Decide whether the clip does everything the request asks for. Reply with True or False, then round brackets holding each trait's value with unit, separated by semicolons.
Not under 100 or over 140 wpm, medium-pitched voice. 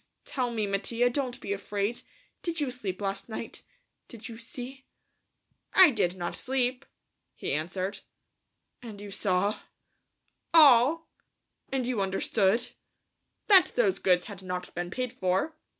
False (135 wpm; 225 Hz)